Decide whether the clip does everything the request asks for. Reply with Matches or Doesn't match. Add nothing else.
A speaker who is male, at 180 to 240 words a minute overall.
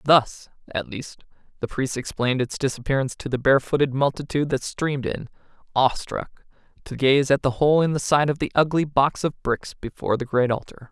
Matches